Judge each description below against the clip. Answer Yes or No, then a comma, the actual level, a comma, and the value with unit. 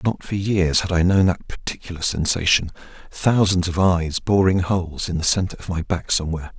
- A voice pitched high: No, very low, 90 Hz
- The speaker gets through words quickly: No, average, 180 wpm